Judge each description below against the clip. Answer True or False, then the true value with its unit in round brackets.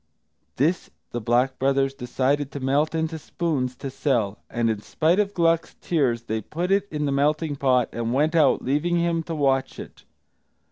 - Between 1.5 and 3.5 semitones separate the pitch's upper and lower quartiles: False (4.1 semitones)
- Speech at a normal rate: True (180 wpm)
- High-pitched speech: False (140 Hz)